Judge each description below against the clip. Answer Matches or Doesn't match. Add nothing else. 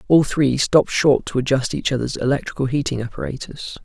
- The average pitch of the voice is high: Doesn't match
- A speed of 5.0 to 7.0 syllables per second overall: Matches